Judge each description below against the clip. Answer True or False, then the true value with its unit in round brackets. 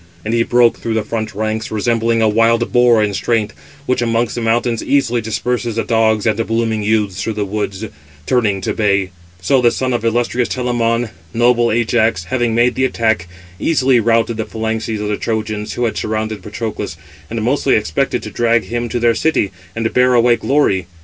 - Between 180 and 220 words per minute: True (190 wpm)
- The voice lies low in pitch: True (115 Hz)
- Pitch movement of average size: False (1.8 semitones)